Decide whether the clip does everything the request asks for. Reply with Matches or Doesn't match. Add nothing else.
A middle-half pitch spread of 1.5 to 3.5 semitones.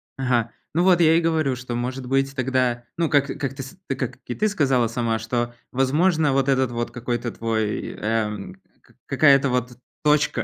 Matches